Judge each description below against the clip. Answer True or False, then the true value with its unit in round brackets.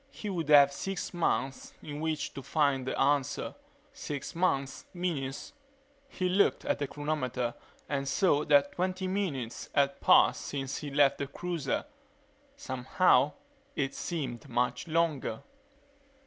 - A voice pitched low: False (145 Hz)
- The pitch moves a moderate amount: True (3.8 semitones)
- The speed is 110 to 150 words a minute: True (135 wpm)